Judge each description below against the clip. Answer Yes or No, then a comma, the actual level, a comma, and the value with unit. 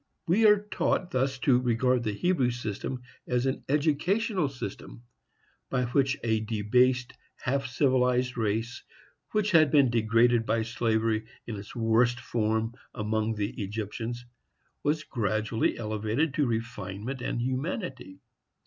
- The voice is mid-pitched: No, low, 120 Hz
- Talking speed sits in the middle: No, slow, 130 wpm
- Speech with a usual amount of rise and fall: Yes, average, 3.5 semitones